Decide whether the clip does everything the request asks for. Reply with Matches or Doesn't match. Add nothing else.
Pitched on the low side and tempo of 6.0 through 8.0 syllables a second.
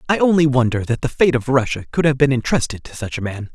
Matches